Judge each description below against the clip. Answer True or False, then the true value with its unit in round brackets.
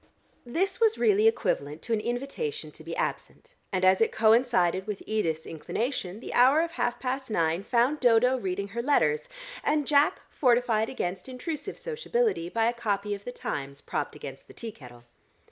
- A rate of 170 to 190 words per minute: True (175 wpm)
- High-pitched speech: True (240 Hz)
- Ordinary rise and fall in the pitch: False (6.8 semitones)